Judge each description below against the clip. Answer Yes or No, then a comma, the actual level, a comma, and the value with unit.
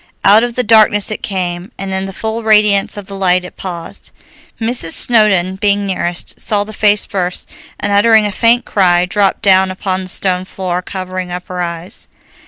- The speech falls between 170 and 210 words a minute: Yes, average, 190 wpm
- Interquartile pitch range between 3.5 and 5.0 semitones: No, narrow, 2.5 semitones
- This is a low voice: No, high, 195 Hz